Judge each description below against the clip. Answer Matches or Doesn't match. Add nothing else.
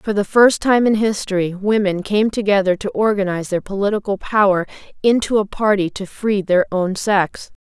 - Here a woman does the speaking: Matches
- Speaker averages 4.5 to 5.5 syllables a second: Matches